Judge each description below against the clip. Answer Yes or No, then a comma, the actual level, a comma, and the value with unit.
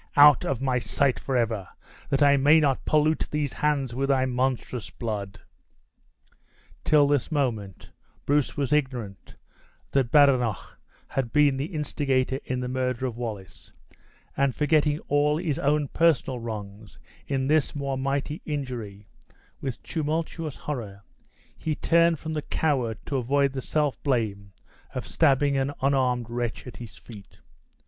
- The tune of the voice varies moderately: Yes, average, 3.4 semitones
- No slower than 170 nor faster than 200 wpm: No, average, 140 wpm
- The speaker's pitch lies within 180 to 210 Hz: No, low, 135 Hz